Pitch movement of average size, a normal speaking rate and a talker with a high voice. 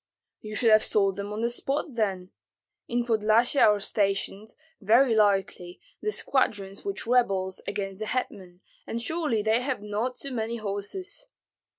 Yes: average, 3.5 semitones; average, 155 wpm; high, 215 Hz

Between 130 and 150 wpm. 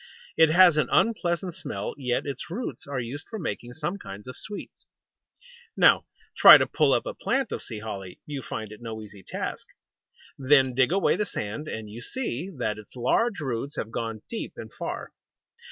No: average, 185 wpm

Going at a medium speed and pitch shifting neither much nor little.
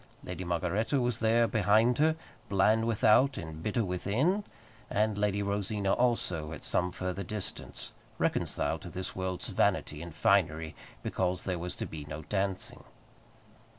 Yes: average, 145 wpm; average, 3.7 semitones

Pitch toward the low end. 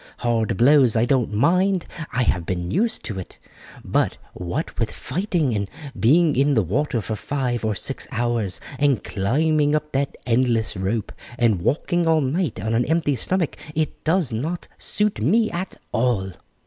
Yes: low, 130 Hz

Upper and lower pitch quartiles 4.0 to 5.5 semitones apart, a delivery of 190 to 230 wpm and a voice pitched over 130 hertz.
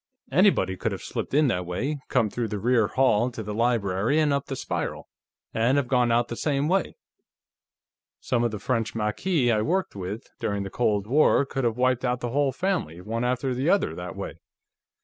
No: average, 4.4 semitones; average, 200 wpm; low, 125 Hz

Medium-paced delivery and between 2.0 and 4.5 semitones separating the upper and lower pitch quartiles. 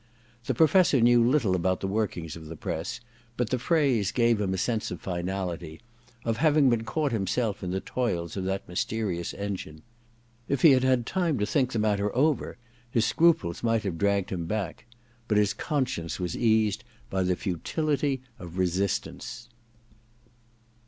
No: average, 170 wpm; average, 5.2 semitones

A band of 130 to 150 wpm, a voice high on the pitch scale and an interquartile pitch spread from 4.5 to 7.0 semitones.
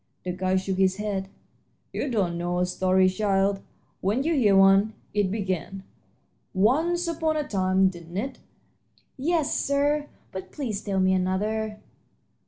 Yes: average, 145 wpm; high, 195 Hz; average, 5.2 semitones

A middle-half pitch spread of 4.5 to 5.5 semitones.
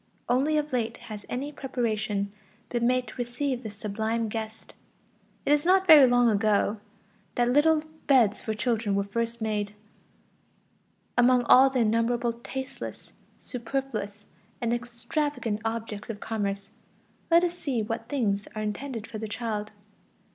No: average, 3.3 semitones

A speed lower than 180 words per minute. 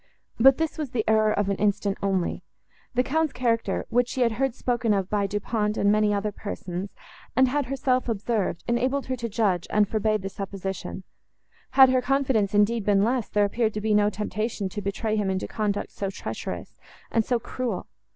No: average, 195 wpm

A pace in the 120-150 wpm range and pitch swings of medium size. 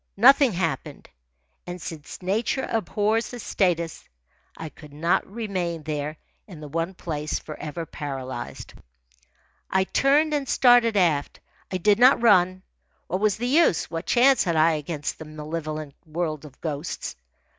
No: average, 145 wpm; wide, 5.7 semitones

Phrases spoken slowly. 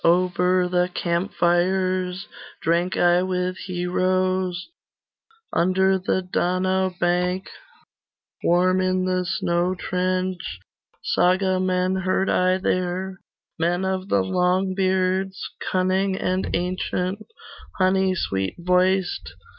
Yes: slow, 95 wpm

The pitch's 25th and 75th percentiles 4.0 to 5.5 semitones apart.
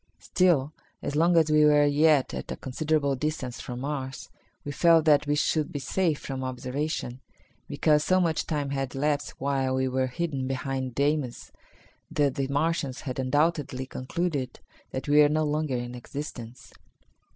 No: narrow, 2.6 semitones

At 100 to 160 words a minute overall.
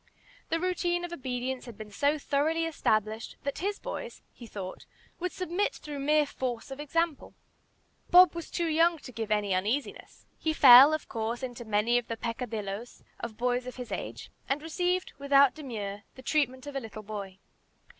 No: average, 175 wpm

